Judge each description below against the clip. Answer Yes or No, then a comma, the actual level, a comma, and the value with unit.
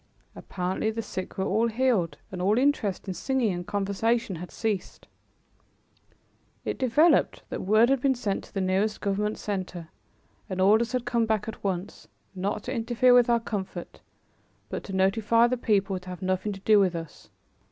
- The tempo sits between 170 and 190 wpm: Yes, average, 175 wpm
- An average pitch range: Yes, average, 3.6 semitones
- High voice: Yes, high, 210 Hz